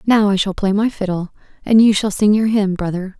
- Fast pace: Yes, fast, 245 wpm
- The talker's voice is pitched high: Yes, high, 205 Hz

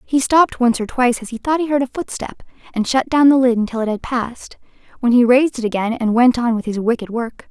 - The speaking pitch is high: Yes, high, 245 Hz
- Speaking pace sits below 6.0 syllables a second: No, 6.2 syllables/s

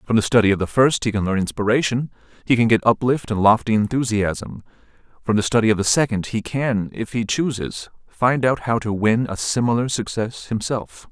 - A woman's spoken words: No, male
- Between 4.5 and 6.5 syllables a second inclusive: Yes, 5.3 syllables/s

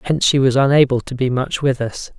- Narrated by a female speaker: No, male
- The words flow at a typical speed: No, fast, 245 wpm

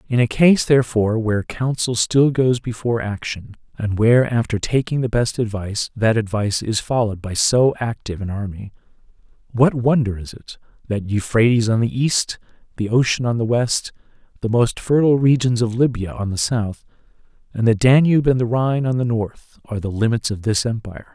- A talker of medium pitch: No, low, 115 Hz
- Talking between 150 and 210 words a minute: Yes, average, 180 wpm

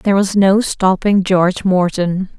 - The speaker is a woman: Yes, female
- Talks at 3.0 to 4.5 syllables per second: Yes, 4.4 syllables/s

